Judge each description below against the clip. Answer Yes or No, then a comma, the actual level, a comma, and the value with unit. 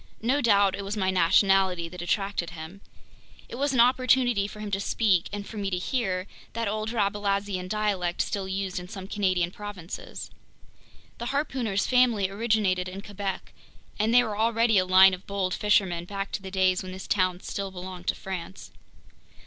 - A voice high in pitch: Yes, high, 195 Hz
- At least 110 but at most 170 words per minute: No, average, 180 wpm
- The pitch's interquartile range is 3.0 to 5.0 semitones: No, narrow, 2.5 semitones